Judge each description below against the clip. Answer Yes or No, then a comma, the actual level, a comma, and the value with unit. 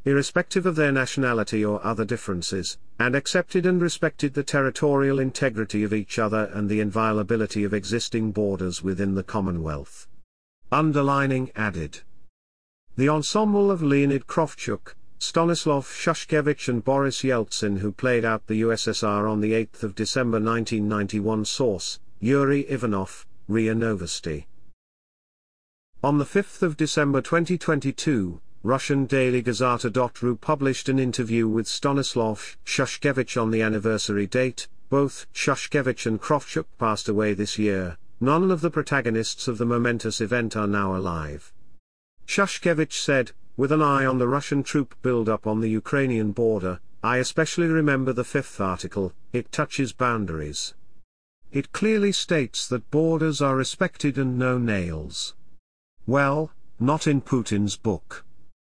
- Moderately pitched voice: No, low, 120 Hz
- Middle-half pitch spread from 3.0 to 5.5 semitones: Yes, average, 5.0 semitones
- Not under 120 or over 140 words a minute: Yes, slow, 135 wpm